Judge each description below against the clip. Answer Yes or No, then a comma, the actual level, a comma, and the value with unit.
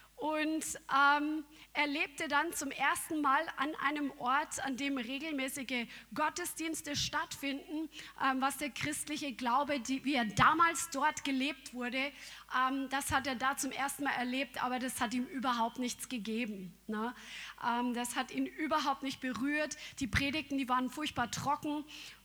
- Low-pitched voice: No, very high, 275 Hz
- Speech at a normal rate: Yes, average, 155 wpm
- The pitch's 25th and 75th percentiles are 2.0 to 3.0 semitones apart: Yes, average, 2.7 semitones